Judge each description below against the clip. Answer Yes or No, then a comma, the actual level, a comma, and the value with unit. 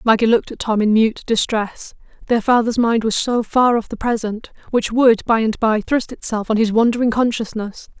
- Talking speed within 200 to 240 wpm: Yes, fast, 205 wpm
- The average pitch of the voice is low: No, high, 225 Hz